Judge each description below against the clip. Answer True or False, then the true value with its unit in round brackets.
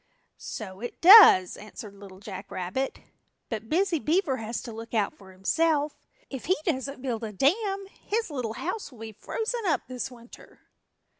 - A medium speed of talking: True (165 wpm)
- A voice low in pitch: False (255 Hz)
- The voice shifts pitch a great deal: True (7.4 semitones)